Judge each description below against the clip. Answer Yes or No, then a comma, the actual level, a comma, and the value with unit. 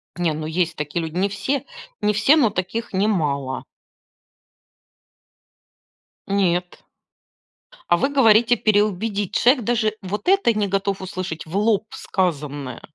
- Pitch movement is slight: No, average, 4.0 semitones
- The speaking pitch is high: Yes, high, 195 Hz